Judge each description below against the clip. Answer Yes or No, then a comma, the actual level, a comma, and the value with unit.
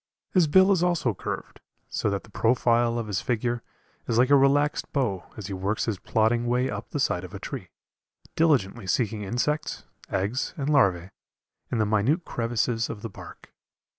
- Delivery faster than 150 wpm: Yes, average, 180 wpm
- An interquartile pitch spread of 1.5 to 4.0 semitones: No, average, 4.7 semitones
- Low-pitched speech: Yes, low, 120 Hz